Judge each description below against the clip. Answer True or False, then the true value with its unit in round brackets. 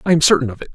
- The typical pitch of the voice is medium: True (145 Hz)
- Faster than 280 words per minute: True (400 wpm)